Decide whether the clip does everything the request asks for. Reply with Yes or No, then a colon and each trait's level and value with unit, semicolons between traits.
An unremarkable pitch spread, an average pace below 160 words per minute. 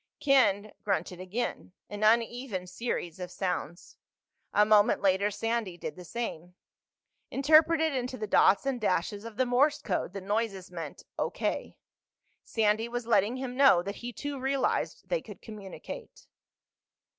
Yes: average, 4.7 semitones; average, 140 wpm